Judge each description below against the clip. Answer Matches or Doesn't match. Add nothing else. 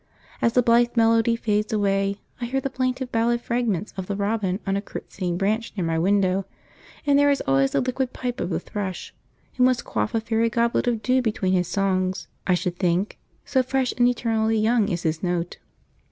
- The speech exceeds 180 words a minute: Matches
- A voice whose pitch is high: Matches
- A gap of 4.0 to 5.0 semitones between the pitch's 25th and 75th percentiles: Matches